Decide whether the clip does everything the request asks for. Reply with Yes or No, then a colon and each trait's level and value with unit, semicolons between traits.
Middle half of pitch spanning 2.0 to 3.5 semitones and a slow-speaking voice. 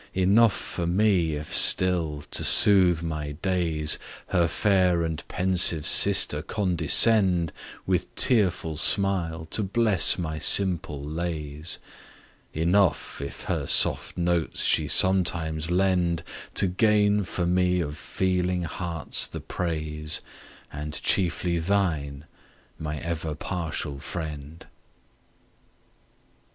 Yes: average, 3.0 semitones; slow, 105 wpm